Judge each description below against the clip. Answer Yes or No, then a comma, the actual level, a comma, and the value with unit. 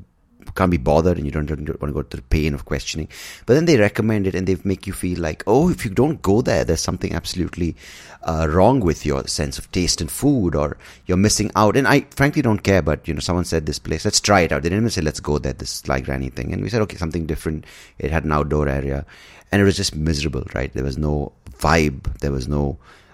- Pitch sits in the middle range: No, very low, 80 Hz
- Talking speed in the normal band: No, fast, 255 wpm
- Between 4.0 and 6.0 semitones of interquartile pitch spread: Yes, average, 4.3 semitones